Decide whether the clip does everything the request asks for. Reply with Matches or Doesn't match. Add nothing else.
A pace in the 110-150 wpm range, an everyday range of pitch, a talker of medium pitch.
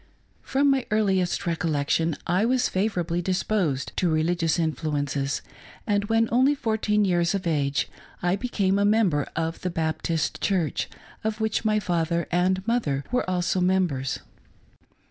Matches